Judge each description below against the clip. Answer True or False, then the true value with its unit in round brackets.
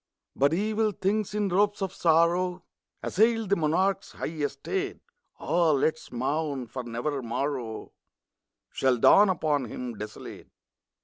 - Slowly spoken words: True (130 wpm)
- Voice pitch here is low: False (160 Hz)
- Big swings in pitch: True (6.6 semitones)